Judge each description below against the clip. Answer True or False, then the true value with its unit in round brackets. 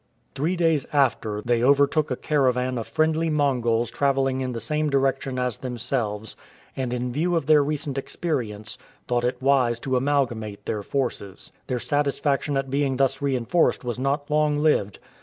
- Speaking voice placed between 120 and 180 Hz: True (135 Hz)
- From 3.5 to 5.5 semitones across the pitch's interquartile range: False (3.1 semitones)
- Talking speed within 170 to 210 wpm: False (160 wpm)